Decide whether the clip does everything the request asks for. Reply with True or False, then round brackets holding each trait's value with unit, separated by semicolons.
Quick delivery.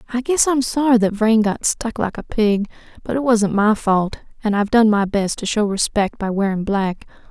True (220 wpm)